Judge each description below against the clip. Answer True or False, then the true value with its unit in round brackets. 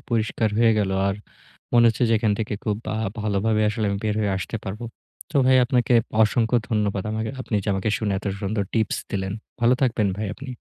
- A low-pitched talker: True (110 Hz)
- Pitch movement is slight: True (2.2 semitones)